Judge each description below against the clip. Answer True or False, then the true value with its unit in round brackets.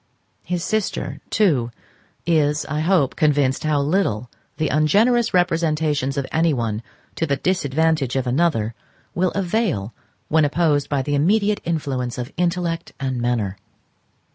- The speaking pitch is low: False (150 Hz)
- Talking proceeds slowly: True (130 wpm)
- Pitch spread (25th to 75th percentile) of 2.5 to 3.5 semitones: False (4.5 semitones)